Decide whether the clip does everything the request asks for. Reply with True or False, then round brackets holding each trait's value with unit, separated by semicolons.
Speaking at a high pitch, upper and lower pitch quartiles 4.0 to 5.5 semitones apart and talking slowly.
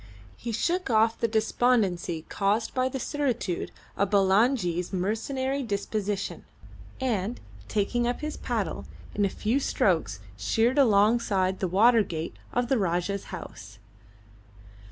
True (215 Hz; 4.3 semitones; 125 wpm)